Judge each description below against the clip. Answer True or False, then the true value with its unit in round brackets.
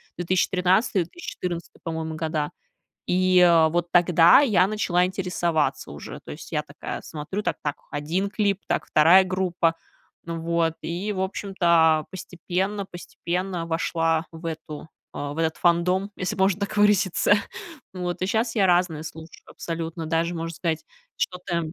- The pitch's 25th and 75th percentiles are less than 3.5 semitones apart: True (2.4 semitones)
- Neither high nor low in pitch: True (175 Hz)